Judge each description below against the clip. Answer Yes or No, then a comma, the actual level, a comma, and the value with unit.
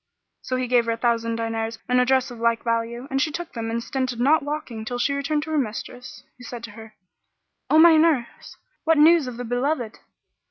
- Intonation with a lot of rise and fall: No, average, 4.0 semitones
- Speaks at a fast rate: Yes, fast, 230 wpm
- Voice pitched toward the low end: No, high, 245 Hz